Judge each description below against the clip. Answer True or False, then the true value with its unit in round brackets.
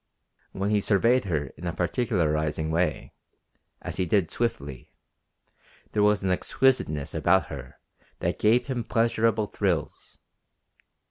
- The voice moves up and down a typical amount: False (6.1 semitones)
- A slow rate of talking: True (125 wpm)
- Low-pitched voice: True (95 Hz)